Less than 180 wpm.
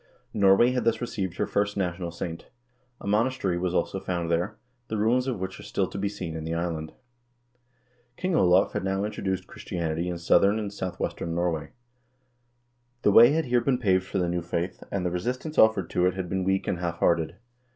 No: fast, 205 wpm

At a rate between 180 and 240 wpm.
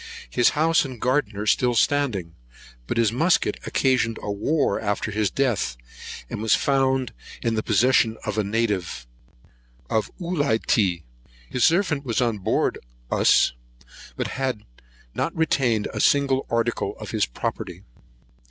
No: average, 145 wpm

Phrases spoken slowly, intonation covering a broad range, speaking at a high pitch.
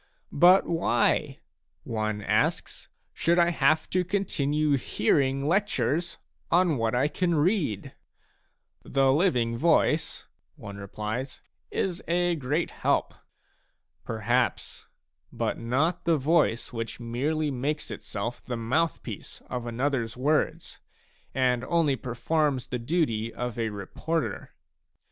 No: slow, 125 wpm; wide, 5.7 semitones; low, 135 Hz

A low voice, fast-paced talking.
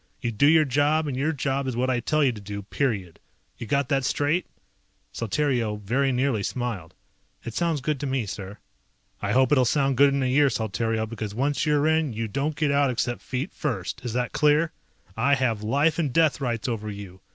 Yes: low, 130 Hz; fast, 210 wpm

